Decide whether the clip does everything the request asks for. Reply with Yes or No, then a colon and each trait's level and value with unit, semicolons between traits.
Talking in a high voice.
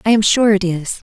Yes: high, 205 Hz